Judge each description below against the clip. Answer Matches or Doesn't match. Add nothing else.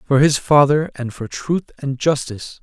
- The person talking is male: Matches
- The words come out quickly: Doesn't match